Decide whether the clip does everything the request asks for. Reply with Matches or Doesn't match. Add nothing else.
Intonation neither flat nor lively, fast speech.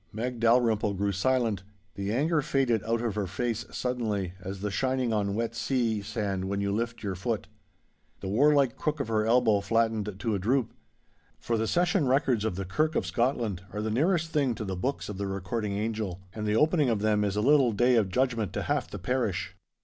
Matches